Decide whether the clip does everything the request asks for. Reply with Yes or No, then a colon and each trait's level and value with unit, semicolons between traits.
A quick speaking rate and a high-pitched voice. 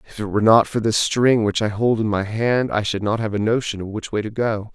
No: fast, 290 wpm; low, 110 Hz